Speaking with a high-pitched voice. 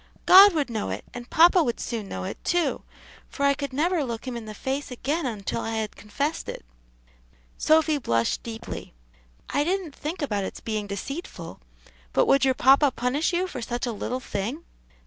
Yes: very high, 265 Hz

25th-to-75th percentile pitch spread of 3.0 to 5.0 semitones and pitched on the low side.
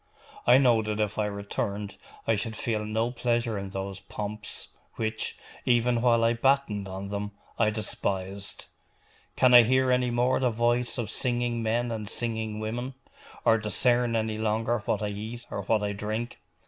No: narrow, 2.4 semitones; low, 110 Hz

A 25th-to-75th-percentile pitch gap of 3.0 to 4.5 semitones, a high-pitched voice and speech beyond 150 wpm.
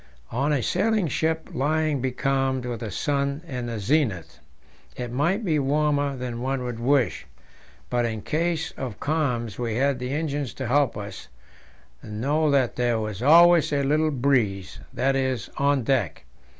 No: average, 3.6 semitones; low, 135 Hz; average, 160 wpm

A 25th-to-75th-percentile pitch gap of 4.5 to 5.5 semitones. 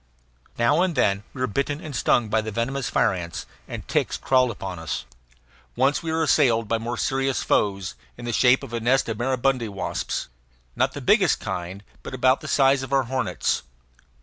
No: average, 3.6 semitones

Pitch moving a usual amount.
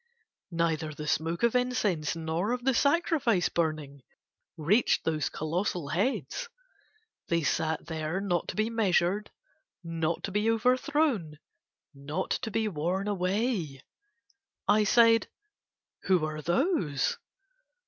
No: wide, 6.1 semitones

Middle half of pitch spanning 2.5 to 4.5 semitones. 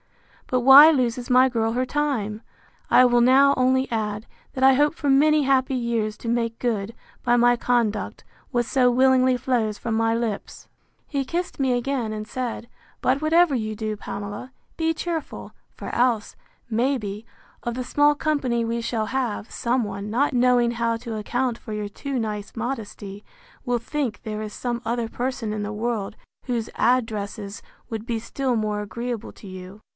Yes: average, 3.1 semitones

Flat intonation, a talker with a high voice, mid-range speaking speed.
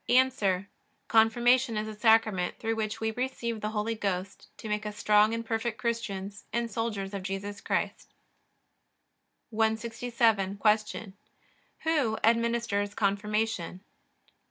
No: narrow, 2.1 semitones; high, 220 Hz; slow, 120 wpm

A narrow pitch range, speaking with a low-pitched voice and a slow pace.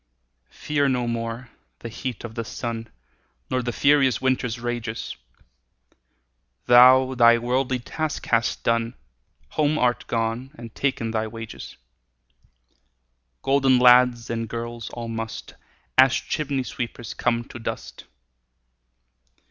Yes: narrow, 2.0 semitones; low, 120 Hz; slow, 115 wpm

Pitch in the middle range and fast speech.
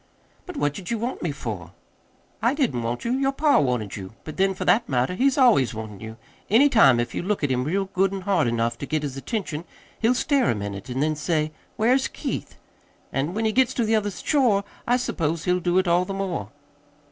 Yes: medium, 180 Hz; fast, 230 wpm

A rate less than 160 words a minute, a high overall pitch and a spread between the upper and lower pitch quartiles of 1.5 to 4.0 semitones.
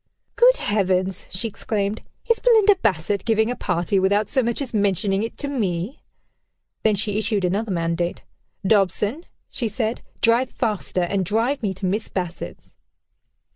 Yes: average, 150 wpm; high, 210 Hz; average, 3.6 semitones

